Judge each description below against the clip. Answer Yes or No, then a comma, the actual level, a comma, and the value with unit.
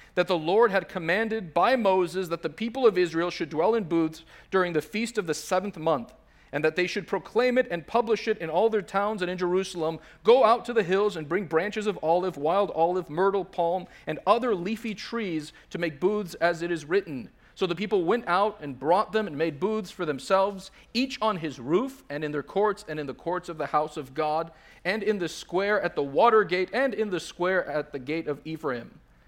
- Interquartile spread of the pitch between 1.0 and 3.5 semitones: No, average, 4.6 semitones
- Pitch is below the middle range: No, medium, 185 Hz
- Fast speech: Yes, fast, 225 wpm